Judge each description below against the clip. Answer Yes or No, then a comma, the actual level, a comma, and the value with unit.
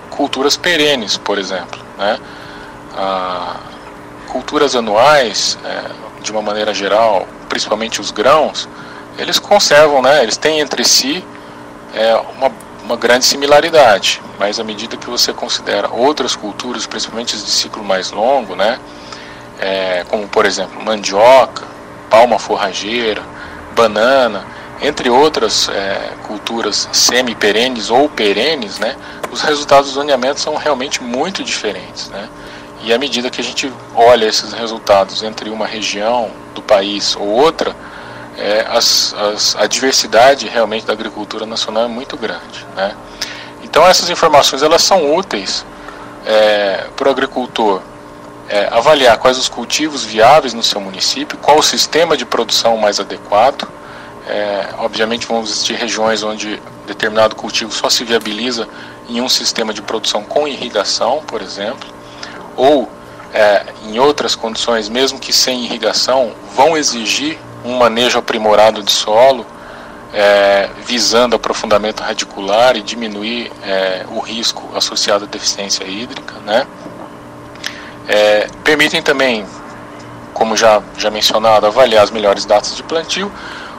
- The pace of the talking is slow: No, average, 135 wpm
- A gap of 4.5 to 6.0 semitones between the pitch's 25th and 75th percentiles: No, average, 3.7 semitones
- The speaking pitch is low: Yes, low, 110 Hz